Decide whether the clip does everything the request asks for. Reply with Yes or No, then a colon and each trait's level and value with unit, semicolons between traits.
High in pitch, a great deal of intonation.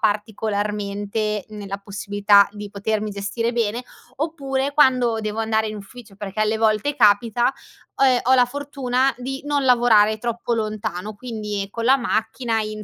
No: high, 220 Hz; average, 3.0 semitones